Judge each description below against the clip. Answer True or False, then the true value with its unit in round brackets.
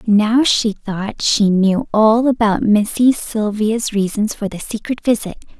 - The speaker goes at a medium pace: True (150 wpm)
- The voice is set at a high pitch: True (215 Hz)